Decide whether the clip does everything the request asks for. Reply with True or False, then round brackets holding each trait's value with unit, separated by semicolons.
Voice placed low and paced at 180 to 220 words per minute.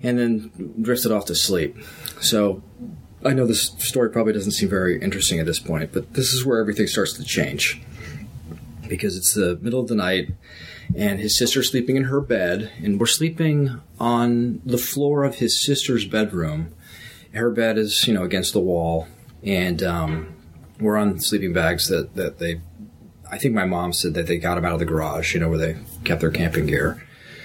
True (105 Hz; 195 wpm)